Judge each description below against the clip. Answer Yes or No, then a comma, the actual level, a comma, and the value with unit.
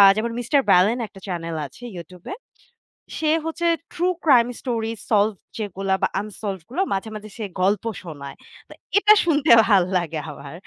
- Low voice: No, high, 210 Hz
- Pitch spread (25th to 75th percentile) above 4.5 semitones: Yes, average, 5.1 semitones